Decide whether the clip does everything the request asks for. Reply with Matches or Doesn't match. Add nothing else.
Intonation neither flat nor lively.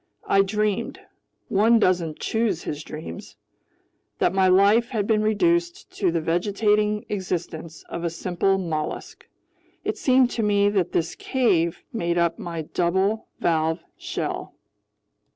Matches